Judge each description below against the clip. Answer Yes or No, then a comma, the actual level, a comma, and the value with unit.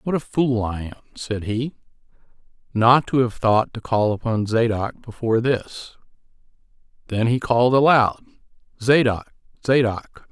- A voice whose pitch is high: No, low, 115 Hz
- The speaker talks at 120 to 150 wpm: Yes, slow, 135 wpm